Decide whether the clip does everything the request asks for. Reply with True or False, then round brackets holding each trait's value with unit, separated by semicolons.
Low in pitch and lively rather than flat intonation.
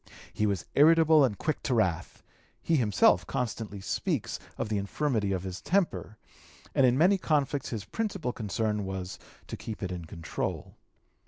True (110 Hz; 7.1 semitones)